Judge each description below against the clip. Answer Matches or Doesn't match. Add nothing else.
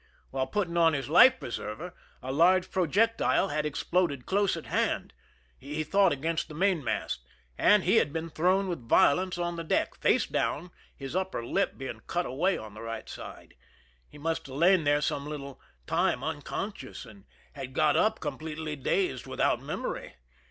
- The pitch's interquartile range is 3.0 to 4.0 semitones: Doesn't match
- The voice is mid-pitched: Matches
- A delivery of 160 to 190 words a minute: Matches